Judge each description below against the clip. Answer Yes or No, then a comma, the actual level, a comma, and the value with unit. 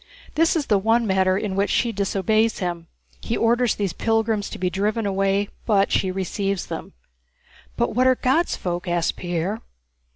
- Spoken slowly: No, average, 170 wpm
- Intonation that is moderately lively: Yes, average, 3.1 semitones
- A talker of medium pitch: No, high, 200 Hz